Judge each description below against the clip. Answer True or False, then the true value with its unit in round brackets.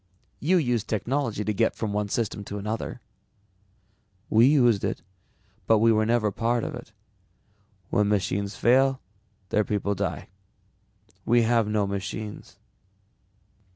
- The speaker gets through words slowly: True (130 wpm)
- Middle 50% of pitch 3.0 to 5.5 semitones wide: False (2.5 semitones)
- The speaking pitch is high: False (110 Hz)